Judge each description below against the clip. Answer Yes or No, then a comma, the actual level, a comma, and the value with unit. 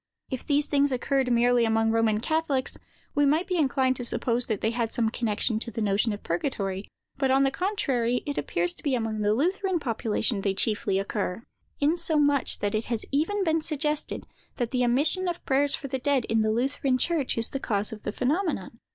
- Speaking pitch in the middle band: No, very high, 250 Hz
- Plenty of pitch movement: No, average, 4.5 semitones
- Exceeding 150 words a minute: Yes, fast, 205 wpm